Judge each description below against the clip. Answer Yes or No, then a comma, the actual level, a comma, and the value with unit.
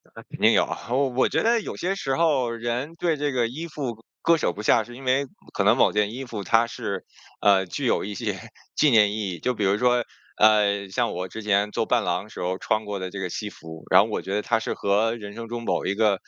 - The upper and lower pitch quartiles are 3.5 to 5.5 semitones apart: Yes, average, 3.9 semitones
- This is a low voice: Yes, low, 110 Hz